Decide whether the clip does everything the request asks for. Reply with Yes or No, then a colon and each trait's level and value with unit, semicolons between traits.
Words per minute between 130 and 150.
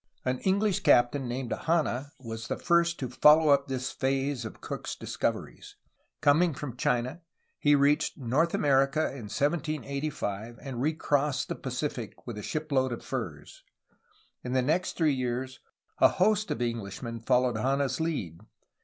Yes: average, 145 wpm